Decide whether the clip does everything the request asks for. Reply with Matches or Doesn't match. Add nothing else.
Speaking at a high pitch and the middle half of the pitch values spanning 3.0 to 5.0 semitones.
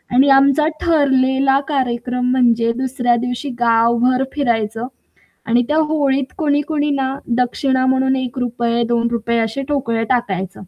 Doesn't match